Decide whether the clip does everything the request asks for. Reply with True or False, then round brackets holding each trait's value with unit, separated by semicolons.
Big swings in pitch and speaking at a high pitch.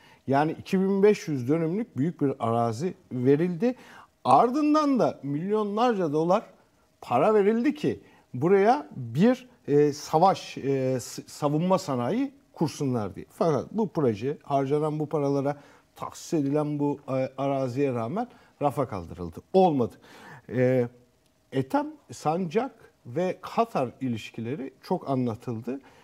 False (6.9 semitones; 145 Hz)